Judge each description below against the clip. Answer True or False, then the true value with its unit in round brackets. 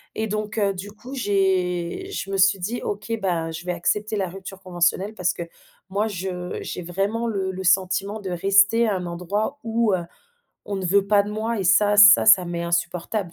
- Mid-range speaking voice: False (195 Hz)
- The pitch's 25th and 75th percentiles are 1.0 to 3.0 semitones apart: True (2.6 semitones)